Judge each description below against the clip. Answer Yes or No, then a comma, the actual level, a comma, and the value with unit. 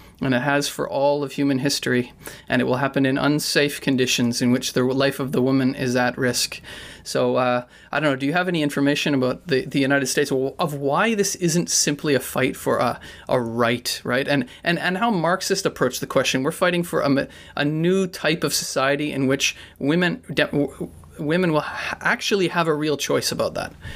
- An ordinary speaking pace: No, fast, 210 wpm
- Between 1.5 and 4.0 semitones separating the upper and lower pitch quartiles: Yes, average, 3.3 semitones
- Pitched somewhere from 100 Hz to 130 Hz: No, medium, 140 Hz